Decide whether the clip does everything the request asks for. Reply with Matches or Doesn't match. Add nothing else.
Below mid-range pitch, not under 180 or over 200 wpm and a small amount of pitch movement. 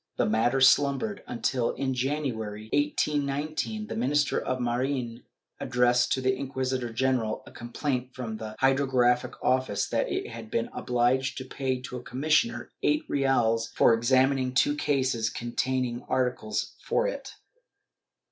Doesn't match